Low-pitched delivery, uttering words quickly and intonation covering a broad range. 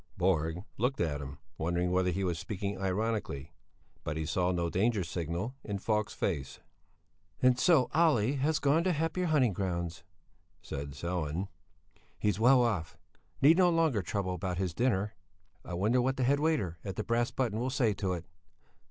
No: low, 100 Hz; average, 170 wpm; wide, 6.6 semitones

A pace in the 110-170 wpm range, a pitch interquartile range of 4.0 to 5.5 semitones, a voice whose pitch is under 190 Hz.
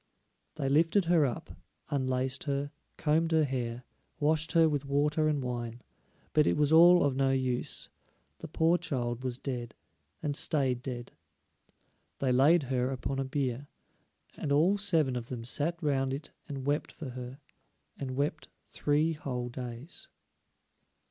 No: average, 150 wpm; average, 3.2 semitones; medium, 140 Hz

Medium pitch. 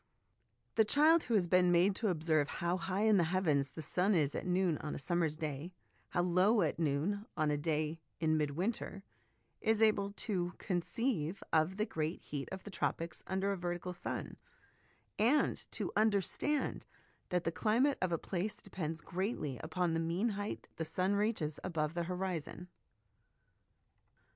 Yes: medium, 180 Hz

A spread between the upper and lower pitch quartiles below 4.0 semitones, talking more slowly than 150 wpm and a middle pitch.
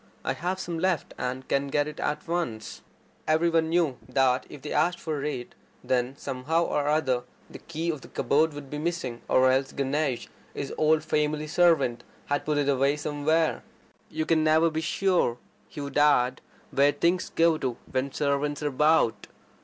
No: average, 2.9 semitones; average, 180 wpm; medium, 150 Hz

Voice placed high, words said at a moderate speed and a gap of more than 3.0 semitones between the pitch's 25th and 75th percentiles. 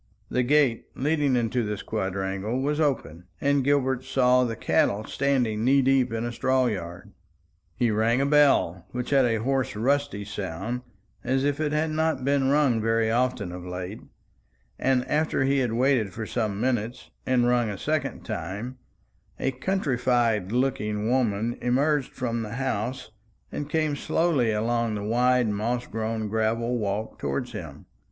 No: low, 120 Hz; average, 160 wpm; average, 3.7 semitones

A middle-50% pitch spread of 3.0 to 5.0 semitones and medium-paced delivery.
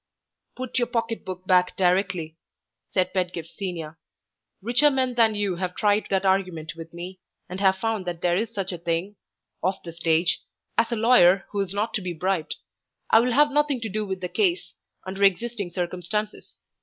Yes: average, 3.9 semitones; average, 185 wpm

